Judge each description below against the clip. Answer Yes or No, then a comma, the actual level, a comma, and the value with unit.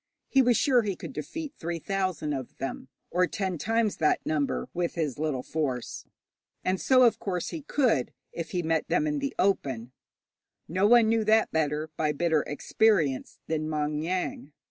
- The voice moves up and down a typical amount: No, wide, 6.4 semitones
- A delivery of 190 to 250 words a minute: No, average, 175 wpm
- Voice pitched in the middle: Yes, medium, 170 Hz